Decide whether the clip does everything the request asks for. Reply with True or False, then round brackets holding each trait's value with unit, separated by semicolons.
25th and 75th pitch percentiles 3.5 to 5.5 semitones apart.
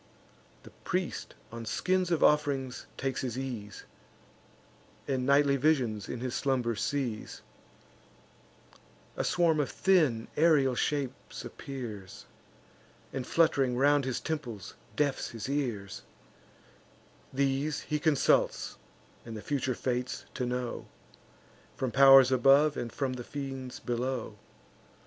False (2.8 semitones)